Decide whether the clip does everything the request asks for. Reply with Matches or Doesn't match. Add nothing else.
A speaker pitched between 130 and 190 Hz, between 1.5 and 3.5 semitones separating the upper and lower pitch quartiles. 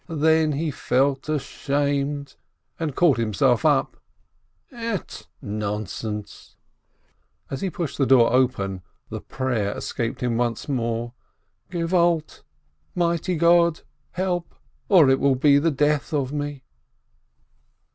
Doesn't match